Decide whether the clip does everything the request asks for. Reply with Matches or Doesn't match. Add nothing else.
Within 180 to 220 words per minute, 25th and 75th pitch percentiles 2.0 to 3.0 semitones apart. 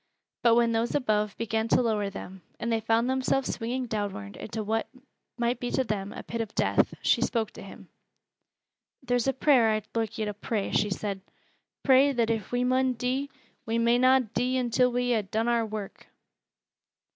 Matches